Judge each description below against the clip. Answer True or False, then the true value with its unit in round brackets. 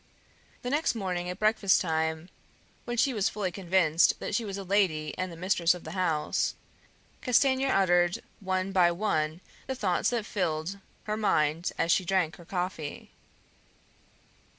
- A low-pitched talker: False (185 Hz)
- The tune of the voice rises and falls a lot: False (3.5 semitones)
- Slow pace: False (155 wpm)